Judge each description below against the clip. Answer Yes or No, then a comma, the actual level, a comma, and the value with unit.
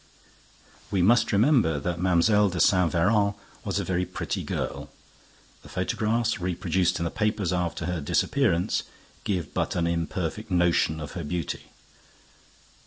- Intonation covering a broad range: No, average, 3.5 semitones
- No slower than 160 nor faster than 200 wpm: No, average, 140 wpm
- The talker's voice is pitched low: Yes, very low, 90 Hz